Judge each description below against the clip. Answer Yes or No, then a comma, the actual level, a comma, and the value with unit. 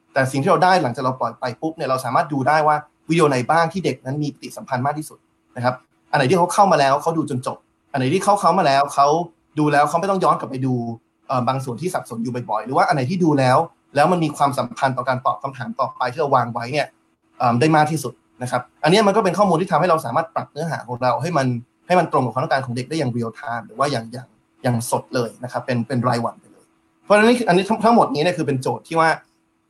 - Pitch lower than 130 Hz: No, medium, 140 Hz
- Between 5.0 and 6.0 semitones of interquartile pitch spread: No, average, 4.6 semitones